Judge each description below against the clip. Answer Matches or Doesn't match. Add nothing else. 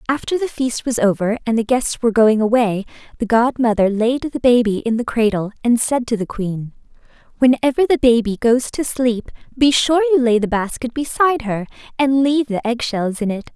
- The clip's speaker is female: Matches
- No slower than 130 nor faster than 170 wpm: Doesn't match